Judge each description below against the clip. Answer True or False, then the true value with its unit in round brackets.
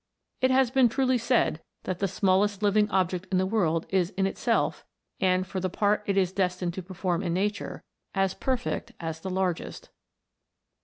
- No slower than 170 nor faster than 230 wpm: True (175 wpm)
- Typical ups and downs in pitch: False (2.3 semitones)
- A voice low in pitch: False (190 Hz)